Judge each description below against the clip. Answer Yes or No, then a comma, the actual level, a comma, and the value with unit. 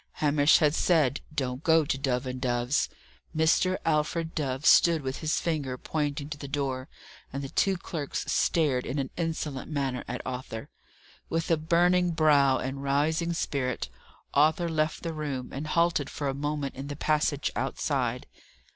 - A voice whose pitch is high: No, medium, 145 Hz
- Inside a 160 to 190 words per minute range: Yes, average, 165 wpm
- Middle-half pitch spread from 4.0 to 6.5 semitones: No, average, 3.1 semitones